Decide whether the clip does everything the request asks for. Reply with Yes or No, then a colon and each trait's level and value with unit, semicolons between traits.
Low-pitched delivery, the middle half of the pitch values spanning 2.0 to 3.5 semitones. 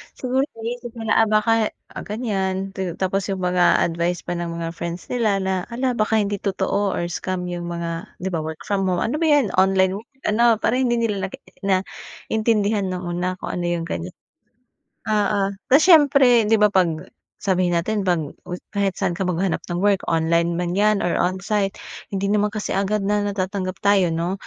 No: high, 195 Hz; average, 3.2 semitones